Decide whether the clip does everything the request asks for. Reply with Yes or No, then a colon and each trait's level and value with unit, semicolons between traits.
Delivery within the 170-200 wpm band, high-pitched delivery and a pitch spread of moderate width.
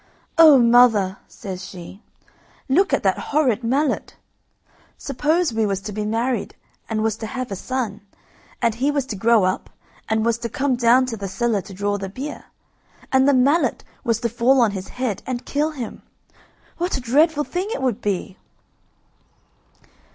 Yes: average, 175 wpm; high, 235 Hz; average, 4.2 semitones